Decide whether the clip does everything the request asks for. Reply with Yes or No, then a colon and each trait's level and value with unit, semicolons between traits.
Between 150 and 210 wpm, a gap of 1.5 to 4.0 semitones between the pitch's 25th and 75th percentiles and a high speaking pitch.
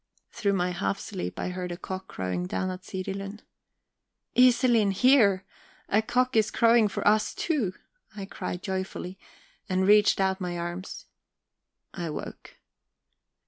No: average, 140 wpm; average, 2.8 semitones; high, 195 Hz